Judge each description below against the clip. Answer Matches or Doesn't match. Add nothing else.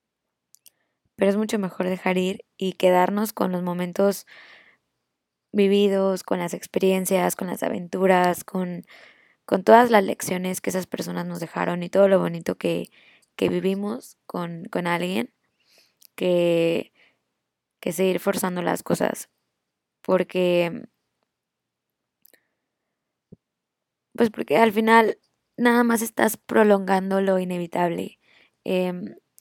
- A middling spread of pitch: Doesn't match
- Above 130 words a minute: Doesn't match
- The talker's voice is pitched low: Doesn't match